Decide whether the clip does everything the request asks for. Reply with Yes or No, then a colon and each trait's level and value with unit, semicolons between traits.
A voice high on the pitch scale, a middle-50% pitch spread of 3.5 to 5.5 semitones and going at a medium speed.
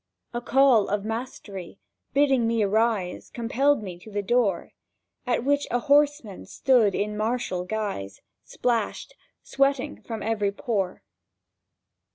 No: high, 225 Hz; average, 3.8 semitones; slow, 120 wpm